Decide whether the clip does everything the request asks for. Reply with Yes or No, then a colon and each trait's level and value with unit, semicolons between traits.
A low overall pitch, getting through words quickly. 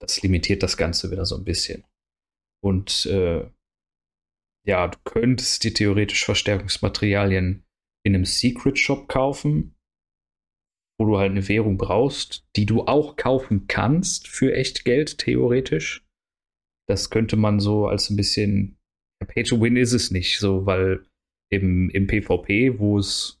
No: low, 100 Hz; average, 140 wpm